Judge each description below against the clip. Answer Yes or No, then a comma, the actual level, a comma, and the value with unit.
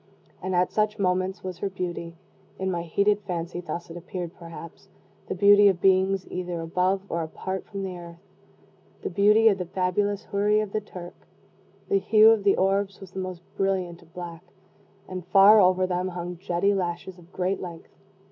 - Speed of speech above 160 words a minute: Yes, average, 185 wpm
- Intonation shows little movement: Yes, narrow, 2.2 semitones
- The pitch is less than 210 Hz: Yes, medium, 185 Hz